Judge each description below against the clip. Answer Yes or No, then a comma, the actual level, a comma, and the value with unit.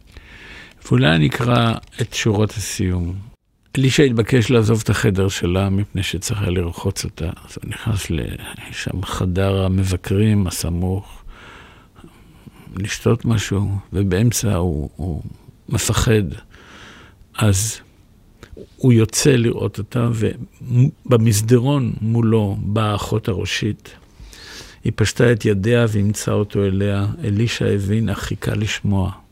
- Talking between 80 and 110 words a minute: Yes, average, 105 wpm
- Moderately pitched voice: No, low, 105 Hz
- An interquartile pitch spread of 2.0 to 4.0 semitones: Yes, average, 3.0 semitones